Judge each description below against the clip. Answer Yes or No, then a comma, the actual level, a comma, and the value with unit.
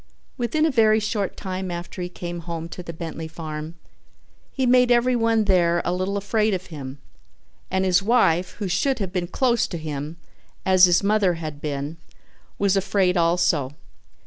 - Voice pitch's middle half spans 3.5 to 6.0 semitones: Yes, average, 4.2 semitones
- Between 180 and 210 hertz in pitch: Yes, medium, 185 Hz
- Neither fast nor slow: Yes, average, 170 wpm